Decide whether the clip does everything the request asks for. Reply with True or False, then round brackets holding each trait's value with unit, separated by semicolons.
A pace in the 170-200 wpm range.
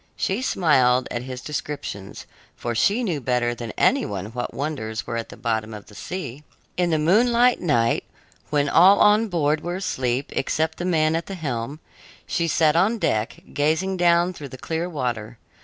True (180 wpm)